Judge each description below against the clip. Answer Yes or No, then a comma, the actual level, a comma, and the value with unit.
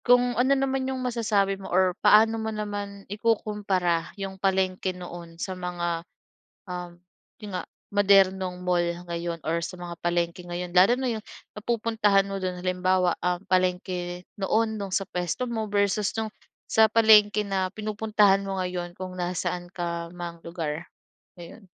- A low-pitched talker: No, high, 190 Hz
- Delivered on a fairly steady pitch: No, average, 3.0 semitones